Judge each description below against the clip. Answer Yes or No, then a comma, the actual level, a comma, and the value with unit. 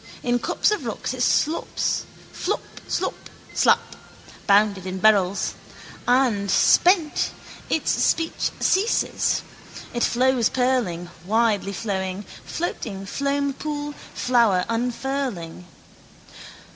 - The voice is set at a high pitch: Yes, high, 235 Hz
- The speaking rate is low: Yes, slow, 95 wpm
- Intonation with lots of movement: Yes, wide, 5.9 semitones